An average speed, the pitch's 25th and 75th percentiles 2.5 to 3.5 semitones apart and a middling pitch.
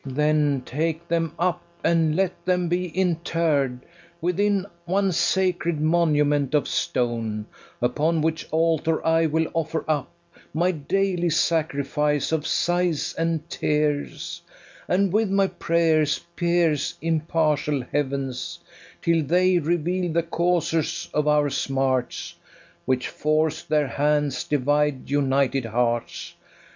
No: slow, 115 wpm; average, 2.8 semitones; medium, 160 Hz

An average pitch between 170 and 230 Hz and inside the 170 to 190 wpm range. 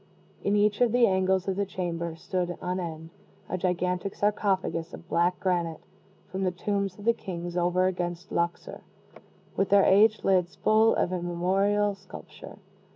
No: medium, 185 Hz; average, 155 wpm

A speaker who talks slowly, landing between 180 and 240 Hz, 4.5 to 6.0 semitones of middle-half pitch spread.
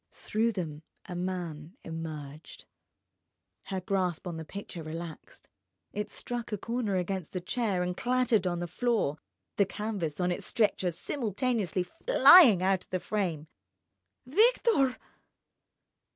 Yes: slow, 125 wpm; medium, 185 Hz; average, 4.9 semitones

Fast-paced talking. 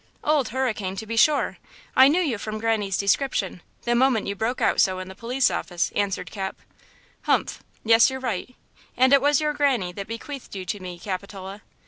No: average, 190 wpm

